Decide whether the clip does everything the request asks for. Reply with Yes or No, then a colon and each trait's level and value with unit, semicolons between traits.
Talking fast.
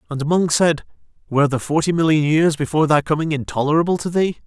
No: average, 190 wpm